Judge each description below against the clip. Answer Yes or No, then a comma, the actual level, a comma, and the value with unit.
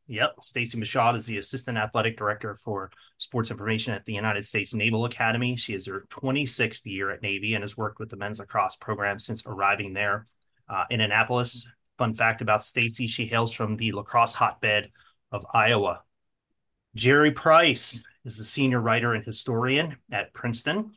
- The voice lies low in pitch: Yes, low, 115 Hz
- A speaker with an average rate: Yes, average, 170 wpm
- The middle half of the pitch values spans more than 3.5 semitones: No, narrow, 2.5 semitones